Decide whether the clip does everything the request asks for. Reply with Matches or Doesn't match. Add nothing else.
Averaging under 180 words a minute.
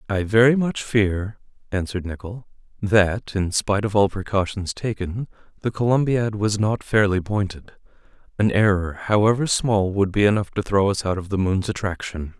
Matches